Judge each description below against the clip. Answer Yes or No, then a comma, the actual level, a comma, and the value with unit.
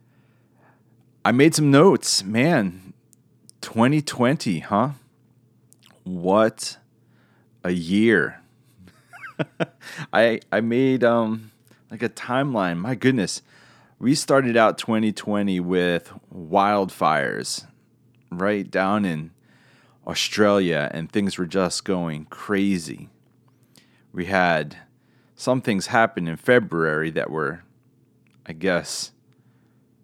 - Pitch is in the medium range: No, low, 110 Hz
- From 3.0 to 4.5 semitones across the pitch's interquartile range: No, average, 4.9 semitones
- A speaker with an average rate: No, slow, 90 wpm